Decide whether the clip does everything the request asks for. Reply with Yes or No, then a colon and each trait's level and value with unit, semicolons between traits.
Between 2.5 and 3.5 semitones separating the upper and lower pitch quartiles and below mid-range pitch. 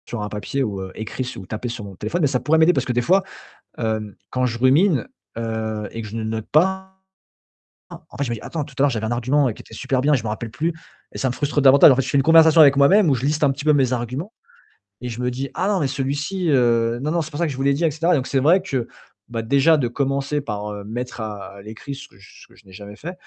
No: average, 4.7 semitones; low, 130 Hz